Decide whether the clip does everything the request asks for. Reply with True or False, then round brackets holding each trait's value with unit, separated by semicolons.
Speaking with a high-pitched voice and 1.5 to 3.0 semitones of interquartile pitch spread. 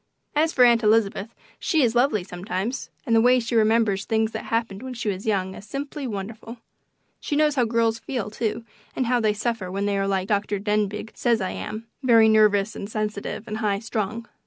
True (220 Hz; 2.6 semitones)